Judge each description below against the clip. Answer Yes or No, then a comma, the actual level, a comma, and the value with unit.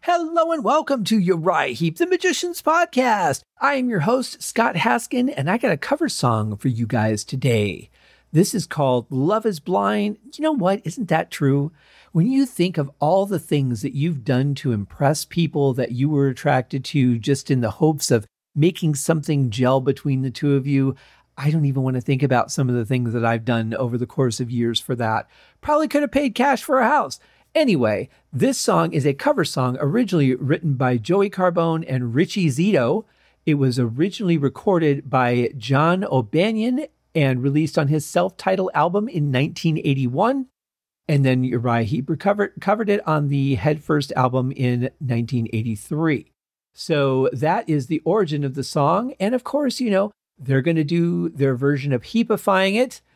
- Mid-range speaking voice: Yes, medium, 150 Hz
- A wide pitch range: Yes, wide, 6.8 semitones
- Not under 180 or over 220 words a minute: Yes, average, 185 wpm